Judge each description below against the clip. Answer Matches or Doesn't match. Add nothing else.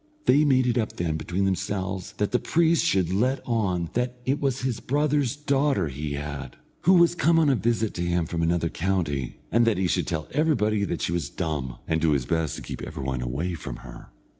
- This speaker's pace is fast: Matches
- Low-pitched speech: Matches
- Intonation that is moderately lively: Doesn't match